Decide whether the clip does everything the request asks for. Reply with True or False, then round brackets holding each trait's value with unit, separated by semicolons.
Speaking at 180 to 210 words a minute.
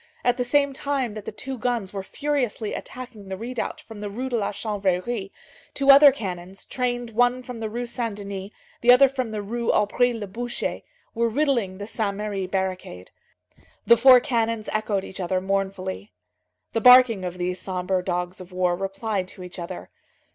True (185 wpm)